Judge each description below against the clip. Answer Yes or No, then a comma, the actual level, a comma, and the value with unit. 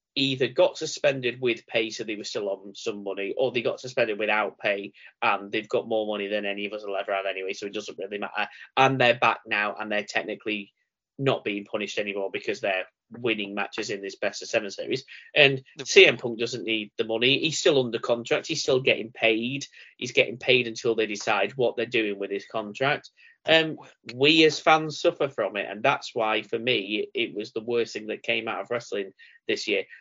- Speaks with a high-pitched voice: No, low, 115 Hz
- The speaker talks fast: Yes, fast, 220 wpm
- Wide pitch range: Yes, wide, 6.0 semitones